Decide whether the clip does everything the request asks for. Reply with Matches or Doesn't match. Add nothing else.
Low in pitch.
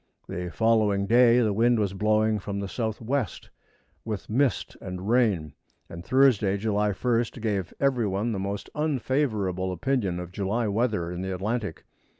Matches